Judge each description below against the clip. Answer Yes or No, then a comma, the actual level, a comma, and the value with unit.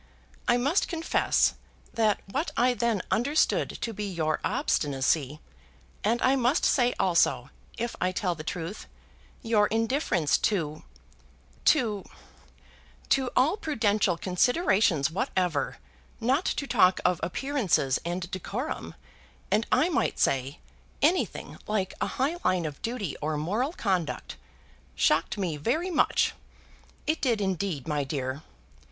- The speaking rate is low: Yes, slow, 125 wpm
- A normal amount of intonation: No, wide, 7.1 semitones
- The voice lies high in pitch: Yes, high, 205 Hz